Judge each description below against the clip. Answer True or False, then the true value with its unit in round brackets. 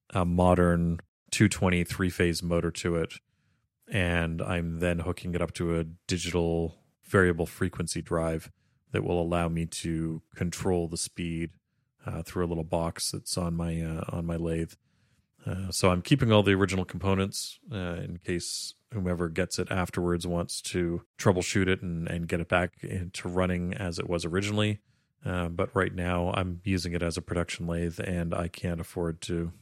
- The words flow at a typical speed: True (175 wpm)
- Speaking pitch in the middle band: False (90 Hz)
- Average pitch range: False (1.6 semitones)